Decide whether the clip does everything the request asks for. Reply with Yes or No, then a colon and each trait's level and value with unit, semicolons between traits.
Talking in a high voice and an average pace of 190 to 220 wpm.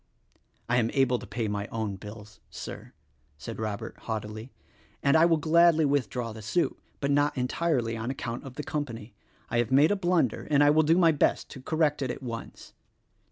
No: low, 130 Hz; average, 200 wpm